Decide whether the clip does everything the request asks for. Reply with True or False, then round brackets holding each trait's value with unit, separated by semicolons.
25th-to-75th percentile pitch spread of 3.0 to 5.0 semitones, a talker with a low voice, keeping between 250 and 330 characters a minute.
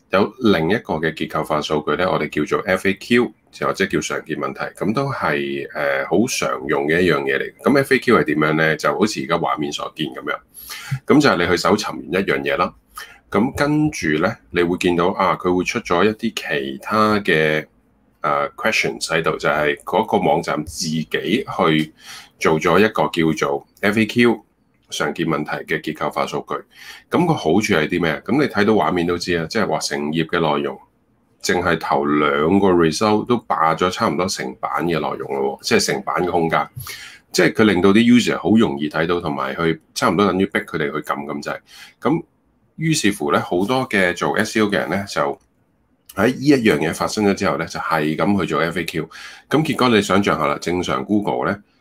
False (5.4 semitones; 90 Hz; 305 characters per minute)